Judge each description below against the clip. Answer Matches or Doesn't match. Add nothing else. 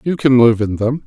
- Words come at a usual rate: Doesn't match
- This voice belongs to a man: Matches